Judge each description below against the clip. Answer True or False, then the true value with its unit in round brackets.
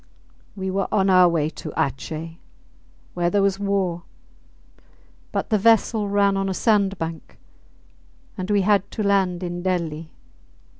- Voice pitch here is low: False (190 Hz)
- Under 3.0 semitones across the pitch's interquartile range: True (2.5 semitones)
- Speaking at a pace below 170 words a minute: True (140 wpm)